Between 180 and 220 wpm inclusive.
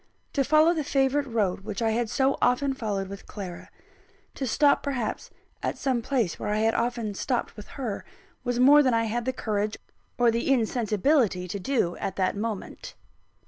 Yes: average, 185 wpm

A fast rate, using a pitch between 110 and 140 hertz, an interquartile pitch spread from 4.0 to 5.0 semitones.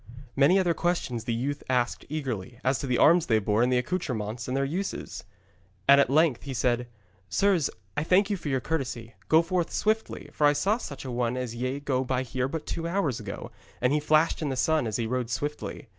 Yes: fast, 220 wpm; low, 135 Hz; average, 4.6 semitones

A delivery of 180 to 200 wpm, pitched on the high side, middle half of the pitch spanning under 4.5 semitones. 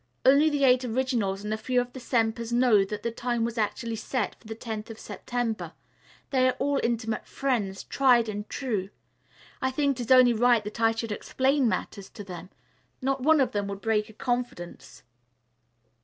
Yes: average, 190 wpm; high, 235 Hz; average, 3.1 semitones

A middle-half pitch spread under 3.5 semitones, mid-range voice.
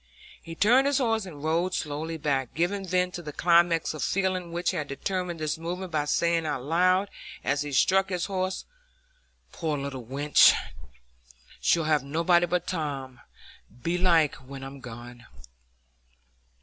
No: average, 3.9 semitones; medium, 165 Hz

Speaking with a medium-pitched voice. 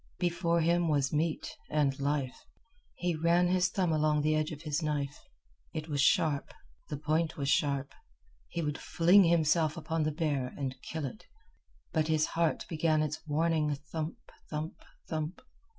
Yes: medium, 155 Hz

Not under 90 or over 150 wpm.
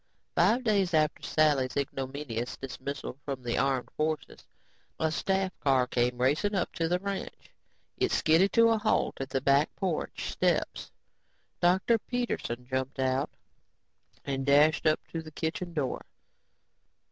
Yes: average, 140 wpm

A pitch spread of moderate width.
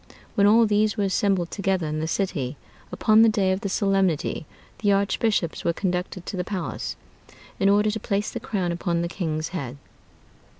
Yes: average, 3.2 semitones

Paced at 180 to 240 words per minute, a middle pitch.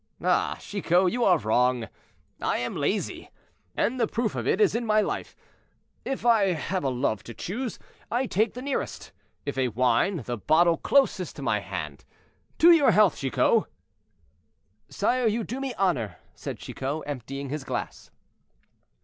No: average, 160 wpm; medium, 180 Hz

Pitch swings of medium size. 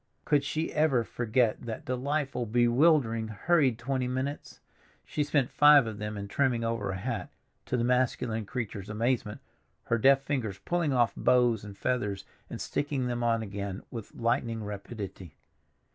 Yes: average, 3.6 semitones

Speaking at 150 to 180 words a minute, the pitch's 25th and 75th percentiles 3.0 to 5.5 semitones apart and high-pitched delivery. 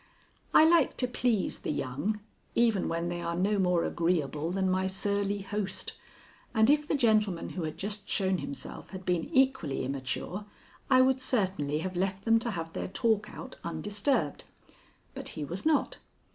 Yes: average, 170 wpm; average, 4.9 semitones; high, 195 Hz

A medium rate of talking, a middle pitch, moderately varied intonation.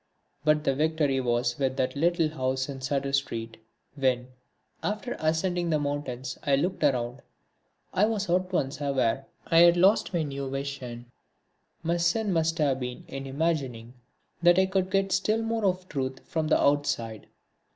Yes: average, 160 wpm; medium, 145 Hz; average, 4.6 semitones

